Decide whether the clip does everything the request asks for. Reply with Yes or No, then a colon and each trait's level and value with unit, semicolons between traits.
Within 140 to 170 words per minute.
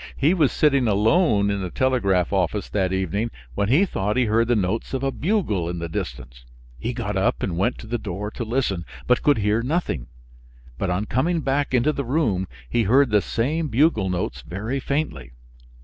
No: average, 195 wpm